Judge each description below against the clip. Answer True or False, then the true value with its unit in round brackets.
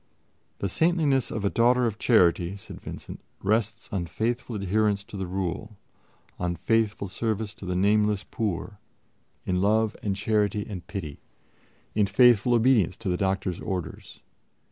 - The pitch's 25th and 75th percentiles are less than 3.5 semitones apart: True (2.8 semitones)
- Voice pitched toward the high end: False (105 Hz)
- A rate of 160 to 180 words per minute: False (145 wpm)